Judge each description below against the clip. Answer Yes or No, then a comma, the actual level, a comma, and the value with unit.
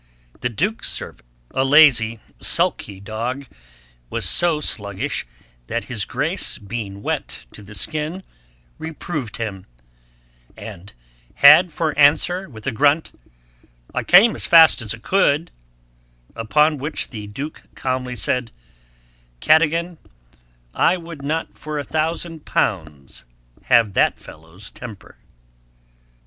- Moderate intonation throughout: No, wide, 6.6 semitones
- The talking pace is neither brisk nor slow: No, slow, 120 wpm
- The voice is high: No, medium, 140 Hz